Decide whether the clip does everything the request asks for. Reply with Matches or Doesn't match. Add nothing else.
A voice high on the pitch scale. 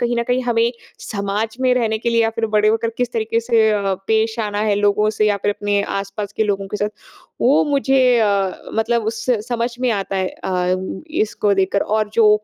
Matches